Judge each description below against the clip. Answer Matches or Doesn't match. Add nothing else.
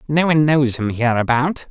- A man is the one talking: Matches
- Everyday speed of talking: Matches